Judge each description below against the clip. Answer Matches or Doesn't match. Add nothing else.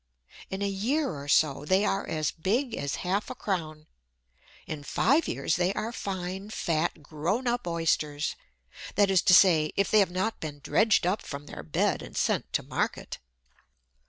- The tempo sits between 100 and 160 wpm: Doesn't match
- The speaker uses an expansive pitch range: Doesn't match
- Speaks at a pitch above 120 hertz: Matches